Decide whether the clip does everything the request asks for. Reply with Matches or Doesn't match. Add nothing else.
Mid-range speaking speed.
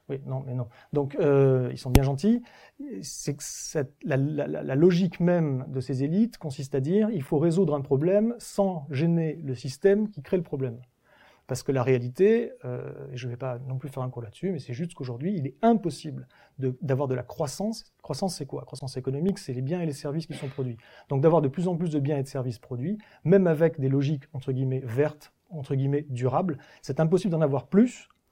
Doesn't match